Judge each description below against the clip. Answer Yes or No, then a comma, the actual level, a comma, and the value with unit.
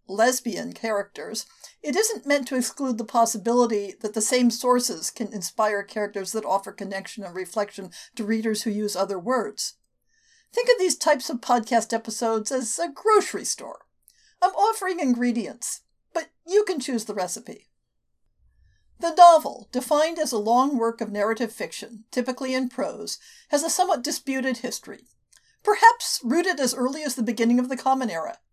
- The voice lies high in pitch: Yes, high, 245 Hz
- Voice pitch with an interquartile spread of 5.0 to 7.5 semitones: Yes, wide, 5.4 semitones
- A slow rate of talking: No, average, 160 wpm